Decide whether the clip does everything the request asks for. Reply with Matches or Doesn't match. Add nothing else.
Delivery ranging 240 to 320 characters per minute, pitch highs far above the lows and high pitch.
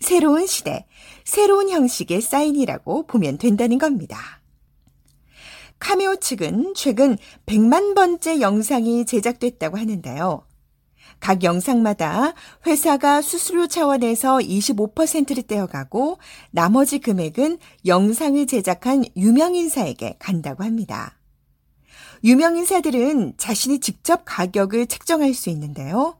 Matches